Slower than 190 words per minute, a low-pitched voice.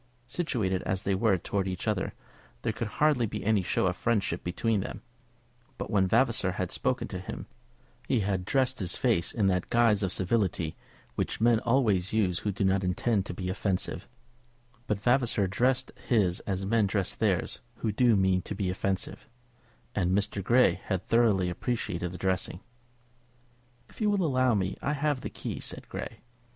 Yes: average, 175 wpm; low, 100 Hz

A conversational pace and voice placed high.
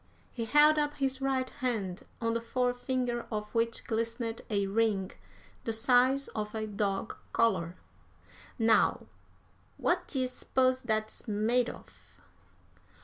No: slow, 125 wpm; high, 230 Hz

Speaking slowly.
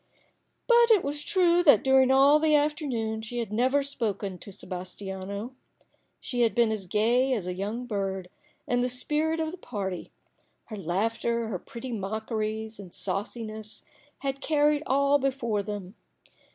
No: average, 160 wpm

